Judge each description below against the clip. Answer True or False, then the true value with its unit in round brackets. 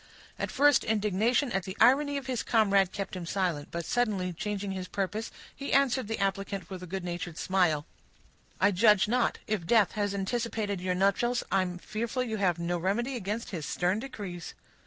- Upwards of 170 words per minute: True (185 wpm)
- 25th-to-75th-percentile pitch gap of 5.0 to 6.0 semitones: False (3.9 semitones)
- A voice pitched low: False (200 Hz)